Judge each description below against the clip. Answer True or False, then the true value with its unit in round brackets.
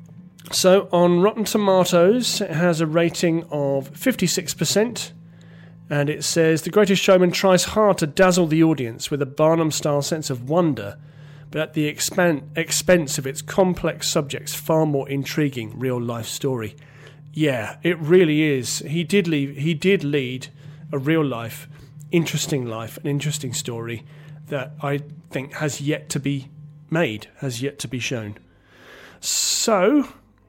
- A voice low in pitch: False (150 Hz)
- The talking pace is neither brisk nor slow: True (150 wpm)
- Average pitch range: True (3.3 semitones)